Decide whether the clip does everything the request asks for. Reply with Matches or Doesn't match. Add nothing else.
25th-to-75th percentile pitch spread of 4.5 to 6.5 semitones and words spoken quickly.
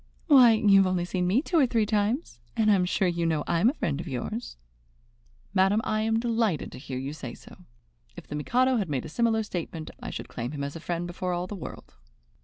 Matches